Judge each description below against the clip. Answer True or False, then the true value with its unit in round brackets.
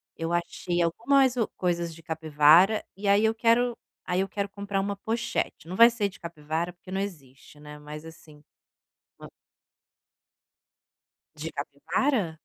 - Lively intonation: False (4.6 semitones)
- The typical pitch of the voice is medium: True (175 Hz)